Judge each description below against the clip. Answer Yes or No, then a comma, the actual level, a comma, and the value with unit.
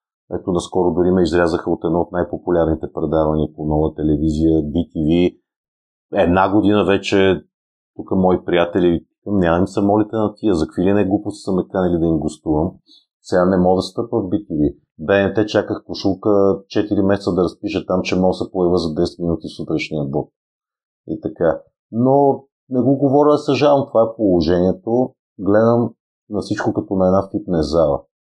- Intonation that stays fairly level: No, average, 3.5 semitones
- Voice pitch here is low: Yes, very low, 95 Hz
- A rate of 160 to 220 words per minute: Yes, fast, 165 wpm